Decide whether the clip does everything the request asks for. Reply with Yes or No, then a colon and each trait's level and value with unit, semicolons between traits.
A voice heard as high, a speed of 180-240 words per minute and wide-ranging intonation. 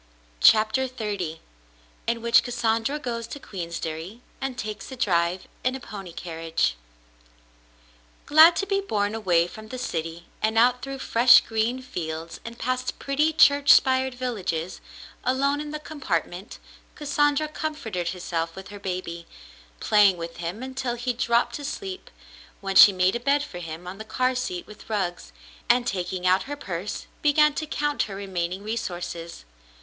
No: high, 220 Hz; average, 155 wpm; wide, 6.6 semitones